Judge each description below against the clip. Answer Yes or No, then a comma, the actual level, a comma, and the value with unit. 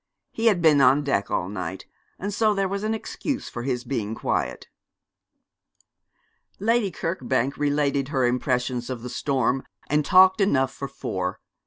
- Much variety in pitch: Yes, wide, 7.1 semitones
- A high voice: No, medium, 140 Hz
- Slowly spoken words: No, average, 155 wpm